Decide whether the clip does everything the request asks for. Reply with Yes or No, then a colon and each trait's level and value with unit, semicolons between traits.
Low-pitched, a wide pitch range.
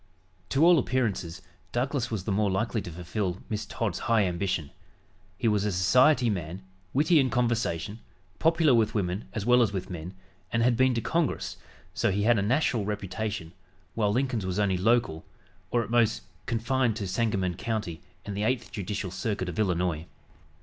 No: low, 105 Hz; average, 4.3 semitones